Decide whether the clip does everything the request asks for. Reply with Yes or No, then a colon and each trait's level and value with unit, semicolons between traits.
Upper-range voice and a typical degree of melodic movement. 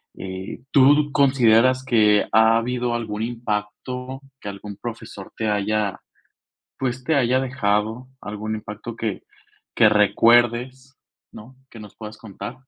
No: low, 115 Hz; average, 3.3 semitones